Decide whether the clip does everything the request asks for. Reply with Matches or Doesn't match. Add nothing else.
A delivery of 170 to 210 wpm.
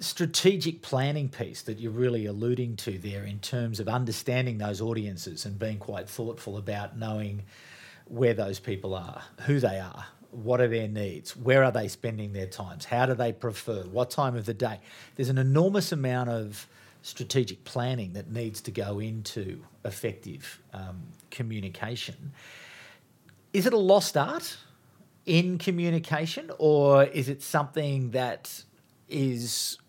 Doesn't match